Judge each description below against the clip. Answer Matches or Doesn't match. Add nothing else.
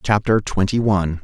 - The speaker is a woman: Doesn't match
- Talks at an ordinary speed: Matches